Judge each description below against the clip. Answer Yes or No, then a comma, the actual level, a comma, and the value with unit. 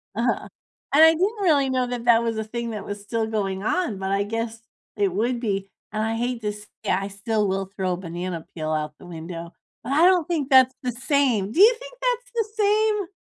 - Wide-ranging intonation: Yes, wide, 7.1 semitones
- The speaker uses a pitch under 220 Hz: No, high, 225 Hz